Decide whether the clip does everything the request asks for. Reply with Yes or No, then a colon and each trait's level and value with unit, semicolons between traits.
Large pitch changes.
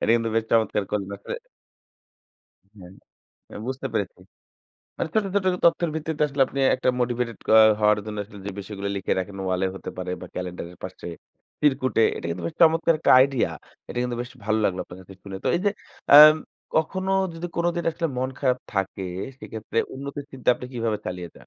Yes: wide, 6.9 semitones